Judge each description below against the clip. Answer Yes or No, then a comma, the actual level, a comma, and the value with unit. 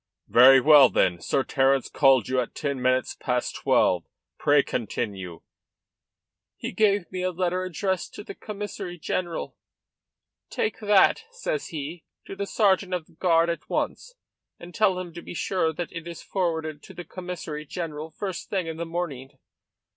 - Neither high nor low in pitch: Yes, medium, 170 Hz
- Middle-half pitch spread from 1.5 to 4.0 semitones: No, average, 4.9 semitones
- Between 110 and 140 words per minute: No, average, 165 wpm